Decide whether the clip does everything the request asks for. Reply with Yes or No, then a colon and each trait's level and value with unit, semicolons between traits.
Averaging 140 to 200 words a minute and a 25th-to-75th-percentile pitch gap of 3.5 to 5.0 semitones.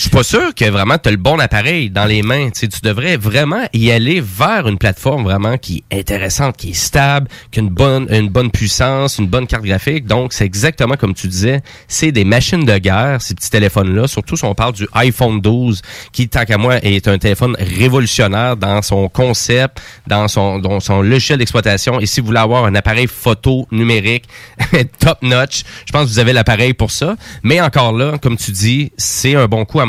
No: fast, 220 wpm; average, 3.9 semitones